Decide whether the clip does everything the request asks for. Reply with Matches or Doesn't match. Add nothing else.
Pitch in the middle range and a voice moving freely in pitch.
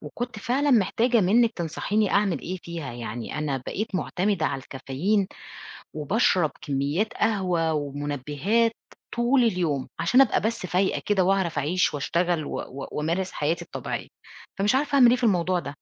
Matches